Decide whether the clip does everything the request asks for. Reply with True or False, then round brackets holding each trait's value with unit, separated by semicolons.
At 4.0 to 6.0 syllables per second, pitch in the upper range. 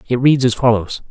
False (5.4 syllables/s; 120 Hz)